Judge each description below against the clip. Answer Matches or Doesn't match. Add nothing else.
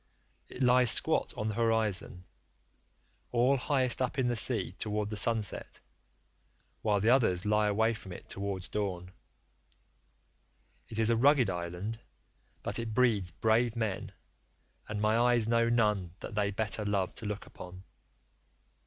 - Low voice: Matches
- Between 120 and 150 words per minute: Matches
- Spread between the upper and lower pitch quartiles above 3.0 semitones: Doesn't match